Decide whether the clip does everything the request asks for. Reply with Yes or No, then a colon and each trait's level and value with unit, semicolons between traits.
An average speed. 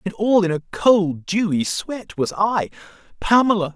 Yes: average, 160 wpm